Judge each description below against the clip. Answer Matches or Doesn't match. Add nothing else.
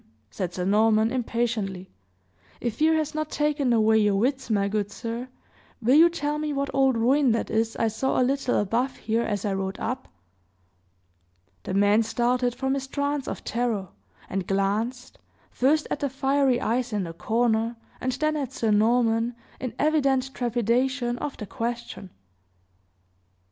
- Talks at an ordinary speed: Matches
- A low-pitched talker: Doesn't match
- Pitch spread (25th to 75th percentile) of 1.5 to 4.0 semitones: Matches